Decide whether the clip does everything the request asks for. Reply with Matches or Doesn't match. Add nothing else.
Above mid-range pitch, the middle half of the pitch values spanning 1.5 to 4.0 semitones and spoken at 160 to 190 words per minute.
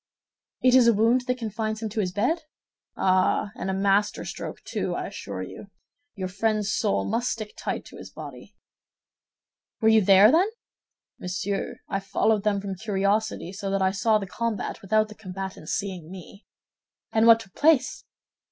Matches